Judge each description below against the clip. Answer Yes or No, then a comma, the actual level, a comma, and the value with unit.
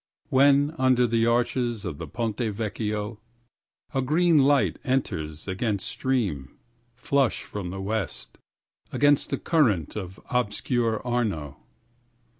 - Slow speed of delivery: Yes, slow, 105 wpm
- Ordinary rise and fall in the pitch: Yes, average, 4.2 semitones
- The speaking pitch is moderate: No, low, 115 Hz